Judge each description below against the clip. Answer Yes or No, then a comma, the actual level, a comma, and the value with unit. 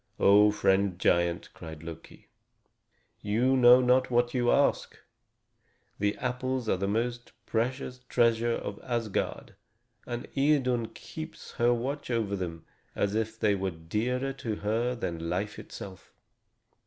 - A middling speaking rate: No, slow, 130 wpm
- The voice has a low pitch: Yes, low, 115 Hz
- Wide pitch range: No, average, 3.8 semitones